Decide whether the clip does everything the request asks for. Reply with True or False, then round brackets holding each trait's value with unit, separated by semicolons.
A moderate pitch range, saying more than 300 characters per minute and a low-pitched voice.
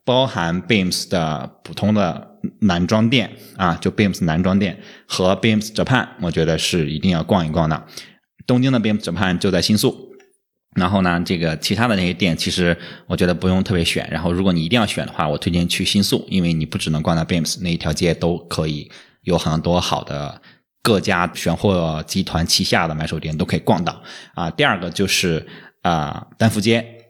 True (4.0 semitones; 335 characters per minute; 90 Hz)